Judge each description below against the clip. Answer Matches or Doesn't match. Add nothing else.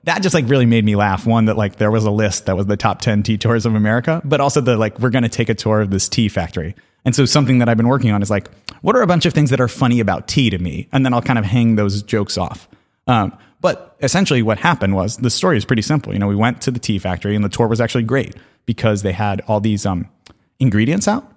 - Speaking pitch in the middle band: Doesn't match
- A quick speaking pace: Matches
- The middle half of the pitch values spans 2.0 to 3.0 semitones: Doesn't match